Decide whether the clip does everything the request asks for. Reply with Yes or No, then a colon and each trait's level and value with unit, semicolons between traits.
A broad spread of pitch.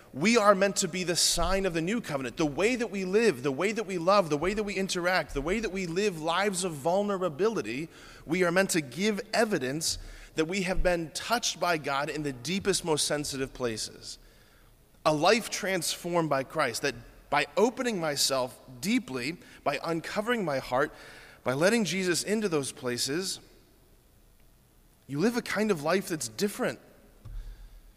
Yes: wide, 5.7 semitones